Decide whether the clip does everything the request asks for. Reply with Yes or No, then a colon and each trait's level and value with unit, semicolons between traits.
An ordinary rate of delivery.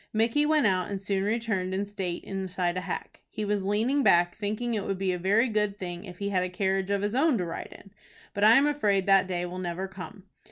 No: fast, 245 wpm